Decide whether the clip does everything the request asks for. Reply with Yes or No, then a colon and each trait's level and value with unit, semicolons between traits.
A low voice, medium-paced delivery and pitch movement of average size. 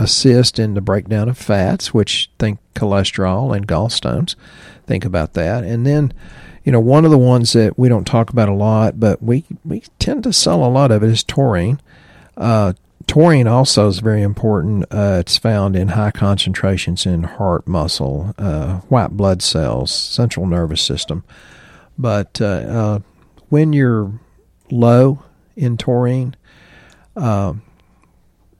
Yes: low, 110 Hz; average, 150 wpm; average, 4.2 semitones